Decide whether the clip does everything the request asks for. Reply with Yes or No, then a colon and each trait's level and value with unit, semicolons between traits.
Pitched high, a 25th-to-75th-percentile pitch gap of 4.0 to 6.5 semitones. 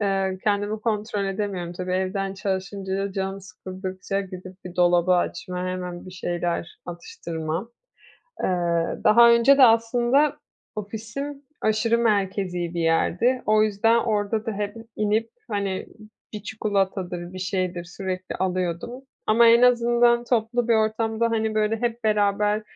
No: high, 205 Hz; average, 3.4 semitones